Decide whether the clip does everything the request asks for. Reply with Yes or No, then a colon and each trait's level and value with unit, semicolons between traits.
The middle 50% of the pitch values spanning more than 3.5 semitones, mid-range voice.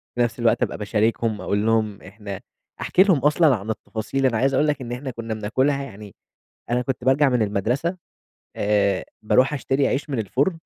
No: average, 4.2 semitones; low, 120 Hz